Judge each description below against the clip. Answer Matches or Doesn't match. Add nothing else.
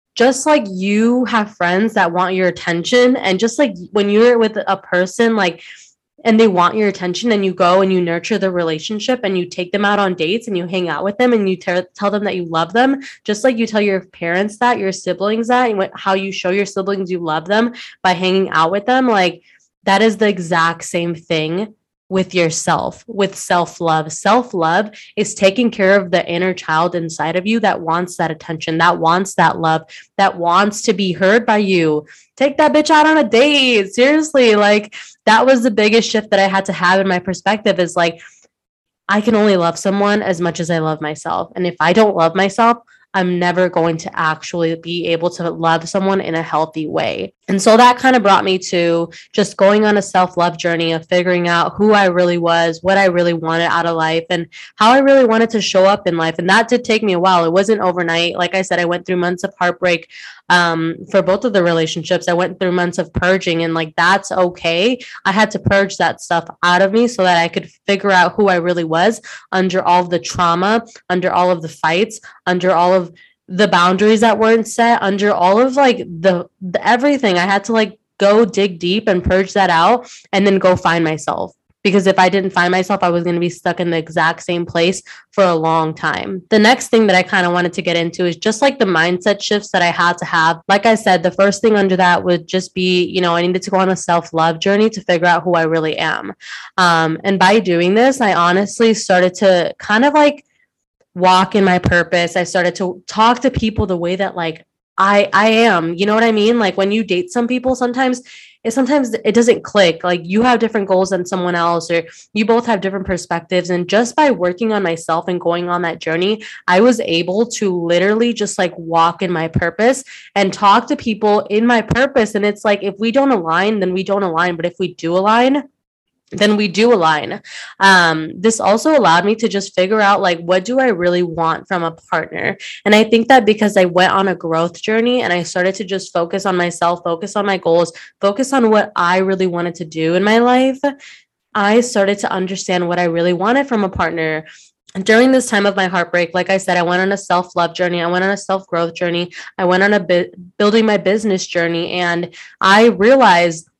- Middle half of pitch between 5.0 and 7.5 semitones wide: Doesn't match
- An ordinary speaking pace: Doesn't match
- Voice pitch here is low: Doesn't match